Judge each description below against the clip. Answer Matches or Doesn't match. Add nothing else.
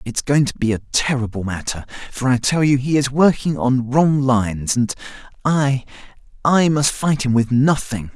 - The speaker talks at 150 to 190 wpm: Matches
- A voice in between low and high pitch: Doesn't match